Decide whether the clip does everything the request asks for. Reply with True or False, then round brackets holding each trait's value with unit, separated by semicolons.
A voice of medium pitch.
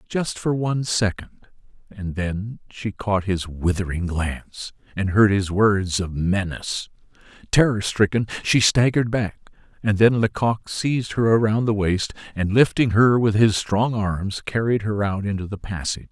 False (105 Hz)